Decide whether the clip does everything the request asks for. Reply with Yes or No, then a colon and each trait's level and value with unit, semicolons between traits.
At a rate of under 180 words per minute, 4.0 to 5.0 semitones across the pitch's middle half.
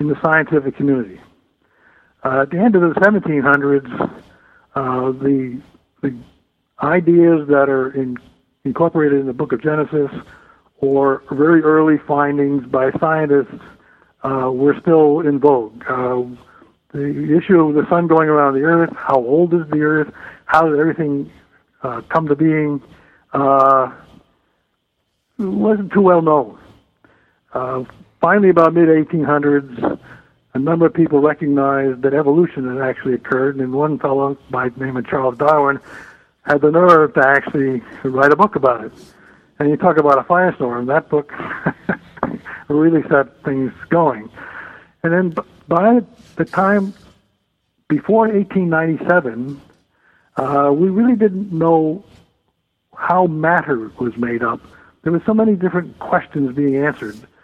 No: average, 140 wpm; average, 3.4 semitones